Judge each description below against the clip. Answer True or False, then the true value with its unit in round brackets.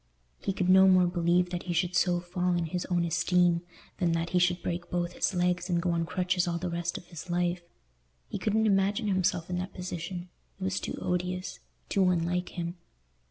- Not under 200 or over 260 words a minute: True (205 wpm)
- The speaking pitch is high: False (180 Hz)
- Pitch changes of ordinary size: False (1.0 semitones)